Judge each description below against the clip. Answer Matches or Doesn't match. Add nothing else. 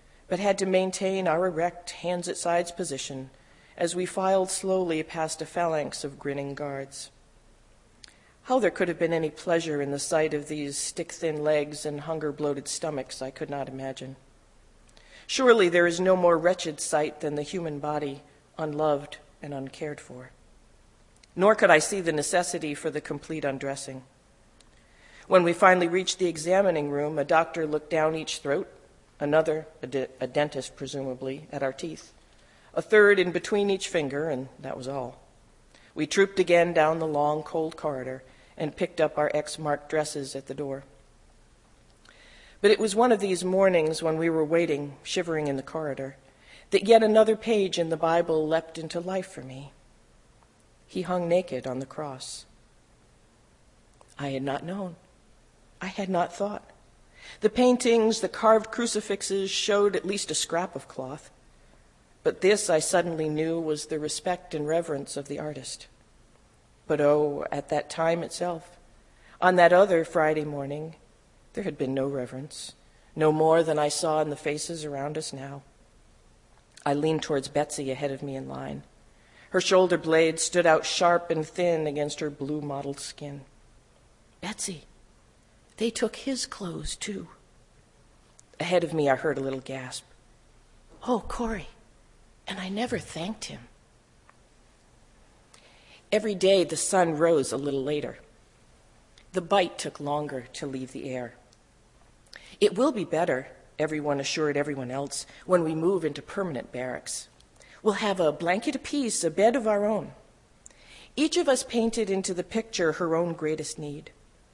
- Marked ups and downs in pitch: Doesn't match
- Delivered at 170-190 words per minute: Doesn't match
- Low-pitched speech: Doesn't match